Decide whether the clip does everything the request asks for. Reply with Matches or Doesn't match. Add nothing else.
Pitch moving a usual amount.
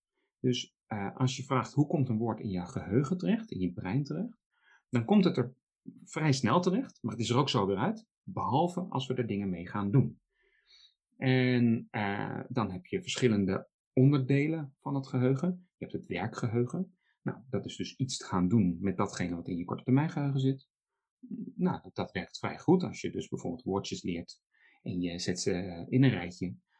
Doesn't match